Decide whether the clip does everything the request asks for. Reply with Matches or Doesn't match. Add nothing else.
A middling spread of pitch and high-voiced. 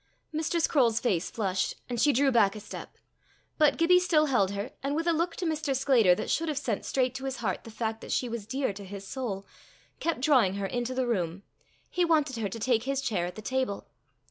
Doesn't match